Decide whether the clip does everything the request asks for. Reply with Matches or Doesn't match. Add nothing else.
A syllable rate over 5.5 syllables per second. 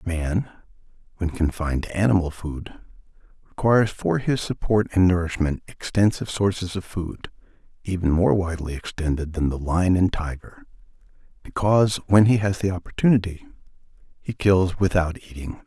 Doesn't match